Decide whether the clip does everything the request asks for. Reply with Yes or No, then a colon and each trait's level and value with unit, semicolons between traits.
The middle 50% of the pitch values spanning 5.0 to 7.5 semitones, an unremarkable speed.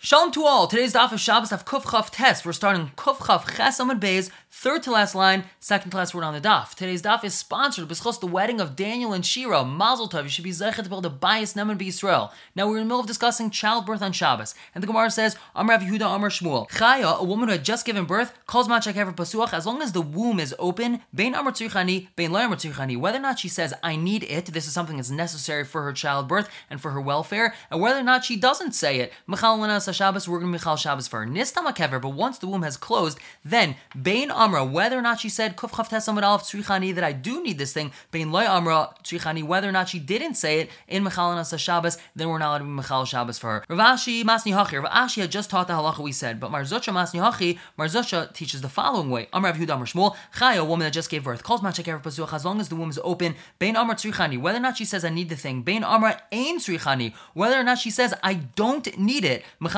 No: wide, 5.5 semitones; fast, 245 wpm